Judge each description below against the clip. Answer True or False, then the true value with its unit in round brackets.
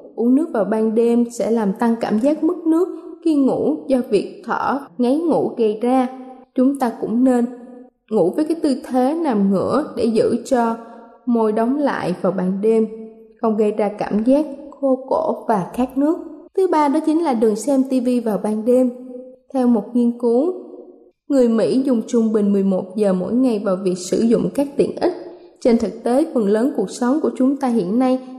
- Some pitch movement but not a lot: True (3.5 semitones)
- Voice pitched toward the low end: False (245 Hz)